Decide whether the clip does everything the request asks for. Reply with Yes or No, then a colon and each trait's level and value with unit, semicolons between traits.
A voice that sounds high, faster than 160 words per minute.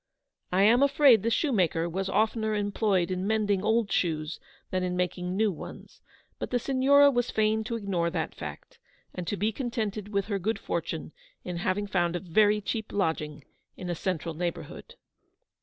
Yes: high, 200 Hz; average, 175 wpm